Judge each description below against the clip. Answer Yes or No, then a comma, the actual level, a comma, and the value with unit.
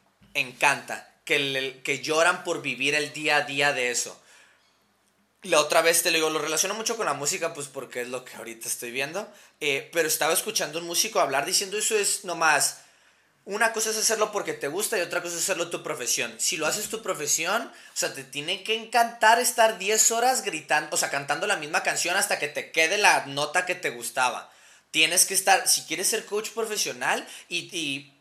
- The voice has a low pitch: No, medium, 165 Hz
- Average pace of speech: No, fast, 210 wpm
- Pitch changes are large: Yes, wide, 5.9 semitones